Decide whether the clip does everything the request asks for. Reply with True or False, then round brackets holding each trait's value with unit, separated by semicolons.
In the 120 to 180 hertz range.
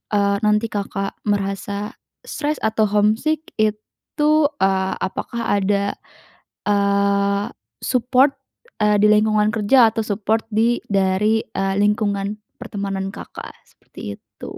False (210 Hz)